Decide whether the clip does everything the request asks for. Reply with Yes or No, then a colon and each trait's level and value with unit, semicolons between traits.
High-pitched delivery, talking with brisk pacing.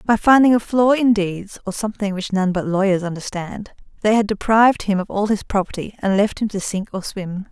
Yes: high, 205 Hz; fast, 225 wpm